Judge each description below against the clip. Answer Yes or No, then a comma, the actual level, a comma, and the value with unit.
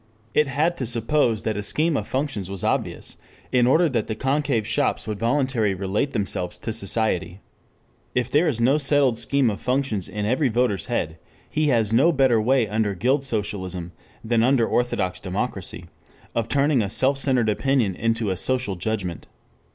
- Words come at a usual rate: Yes, average, 175 wpm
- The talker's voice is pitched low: Yes, low, 115 Hz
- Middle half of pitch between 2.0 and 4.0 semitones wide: No, average, 4.6 semitones